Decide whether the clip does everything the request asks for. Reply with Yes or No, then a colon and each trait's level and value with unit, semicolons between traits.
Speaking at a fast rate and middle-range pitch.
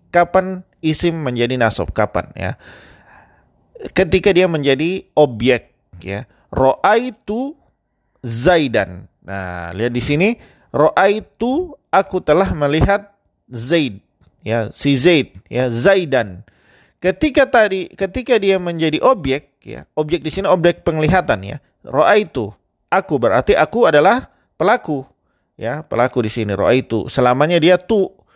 No: average, 125 wpm; medium, 155 Hz